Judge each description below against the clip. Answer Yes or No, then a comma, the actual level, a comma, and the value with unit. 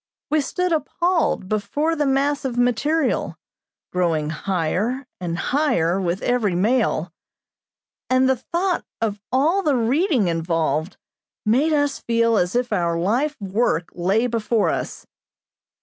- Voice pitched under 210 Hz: No, high, 230 Hz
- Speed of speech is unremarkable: No, slow, 125 wpm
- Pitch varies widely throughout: Yes, wide, 7.8 semitones